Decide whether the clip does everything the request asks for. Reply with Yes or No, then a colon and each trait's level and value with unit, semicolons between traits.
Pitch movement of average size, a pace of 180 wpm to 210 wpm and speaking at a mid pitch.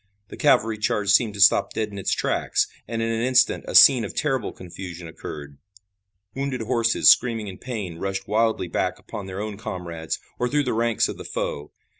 No: average, 3.8 semitones; average, 195 wpm; low, 105 Hz